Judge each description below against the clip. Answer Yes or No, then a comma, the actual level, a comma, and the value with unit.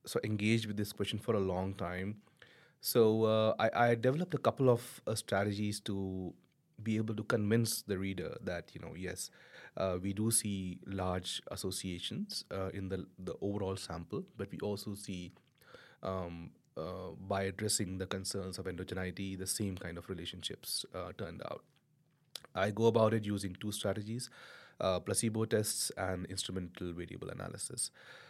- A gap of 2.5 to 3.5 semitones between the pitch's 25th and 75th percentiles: Yes, average, 3.0 semitones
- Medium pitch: No, low, 100 Hz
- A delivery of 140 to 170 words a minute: Yes, average, 160 wpm